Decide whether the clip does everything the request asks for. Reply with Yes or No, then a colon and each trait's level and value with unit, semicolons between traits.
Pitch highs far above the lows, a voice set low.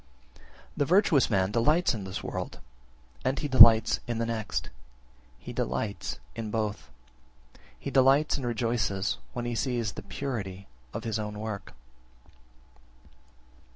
No: average, 3.8 semitones; low, 115 Hz